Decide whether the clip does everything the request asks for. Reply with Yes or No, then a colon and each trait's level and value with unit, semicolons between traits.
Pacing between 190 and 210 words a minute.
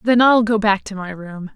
No: fast, 270 wpm